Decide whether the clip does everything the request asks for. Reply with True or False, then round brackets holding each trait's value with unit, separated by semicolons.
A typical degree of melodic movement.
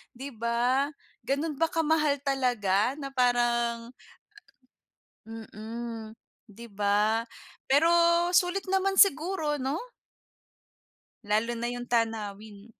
True (4.1 semitones)